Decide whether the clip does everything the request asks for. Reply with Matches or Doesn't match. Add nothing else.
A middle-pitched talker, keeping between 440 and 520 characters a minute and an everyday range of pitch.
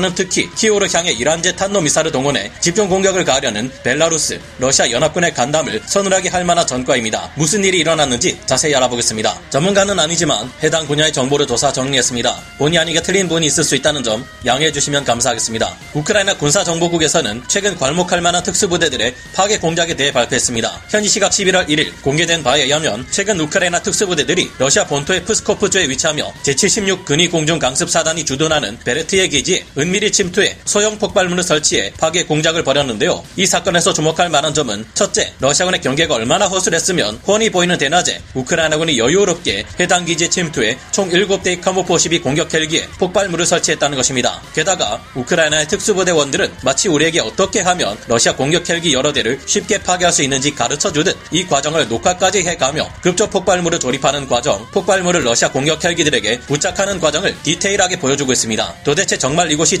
Matches